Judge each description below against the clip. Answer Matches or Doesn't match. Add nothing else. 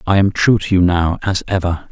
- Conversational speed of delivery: Doesn't match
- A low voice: Matches